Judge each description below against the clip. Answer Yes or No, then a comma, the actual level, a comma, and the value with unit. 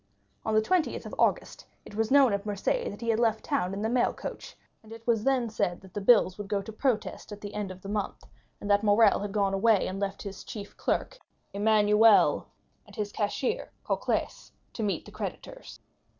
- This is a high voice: Yes, high, 210 Hz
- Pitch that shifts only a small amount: Yes, narrow, 2.0 semitones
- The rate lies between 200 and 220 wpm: Yes, fast, 205 wpm